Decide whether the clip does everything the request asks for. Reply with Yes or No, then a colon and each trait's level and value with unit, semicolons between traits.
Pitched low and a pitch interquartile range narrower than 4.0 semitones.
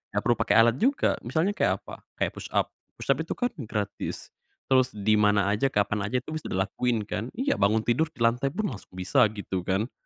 No: low, 115 Hz; average, 4.3 semitones